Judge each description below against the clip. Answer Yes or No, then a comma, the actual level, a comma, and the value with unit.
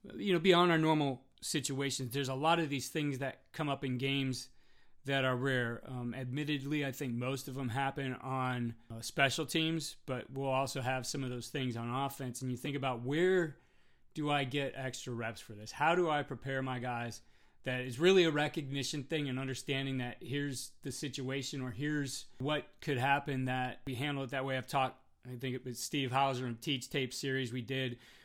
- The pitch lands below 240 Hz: Yes, low, 135 Hz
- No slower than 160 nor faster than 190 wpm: No, fast, 205 wpm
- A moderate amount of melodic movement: No, narrow, 2.1 semitones